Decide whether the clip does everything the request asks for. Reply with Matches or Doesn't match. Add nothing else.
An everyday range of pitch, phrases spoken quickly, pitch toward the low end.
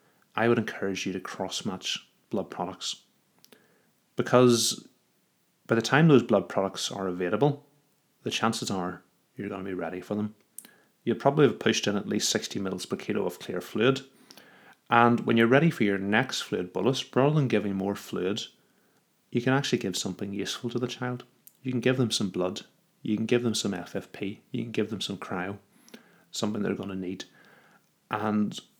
Doesn't match